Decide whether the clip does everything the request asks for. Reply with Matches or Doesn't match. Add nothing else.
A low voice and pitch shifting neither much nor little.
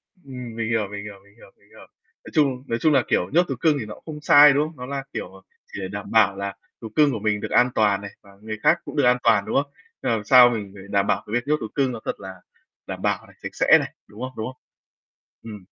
Matches